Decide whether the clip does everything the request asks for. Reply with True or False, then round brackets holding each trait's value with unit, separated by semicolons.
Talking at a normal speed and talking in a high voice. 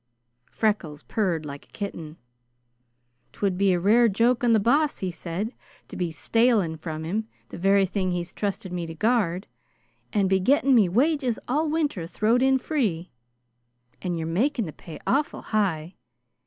True (165 wpm; 200 Hz)